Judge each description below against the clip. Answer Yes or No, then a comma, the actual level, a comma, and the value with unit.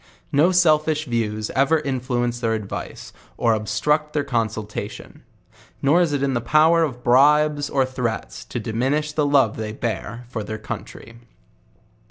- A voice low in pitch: Yes, low, 130 Hz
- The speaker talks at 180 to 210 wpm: No, average, 160 wpm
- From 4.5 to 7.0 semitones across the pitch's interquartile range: Yes, average, 4.8 semitones